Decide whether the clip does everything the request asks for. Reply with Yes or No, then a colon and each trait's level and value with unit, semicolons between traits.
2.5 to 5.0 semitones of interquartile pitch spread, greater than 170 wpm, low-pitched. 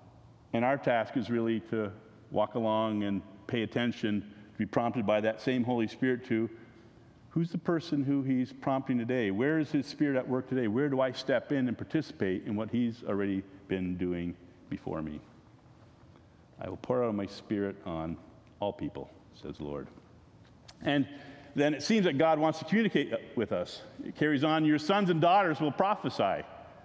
No: wide, 5.5 semitones; average, 185 wpm; low, 120 Hz